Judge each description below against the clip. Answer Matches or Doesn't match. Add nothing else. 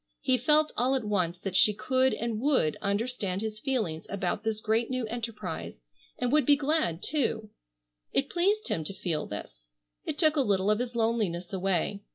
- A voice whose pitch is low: Doesn't match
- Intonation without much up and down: Doesn't match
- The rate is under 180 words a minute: Doesn't match